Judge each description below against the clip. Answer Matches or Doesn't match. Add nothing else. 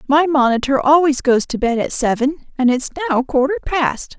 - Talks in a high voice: Matches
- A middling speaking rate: Matches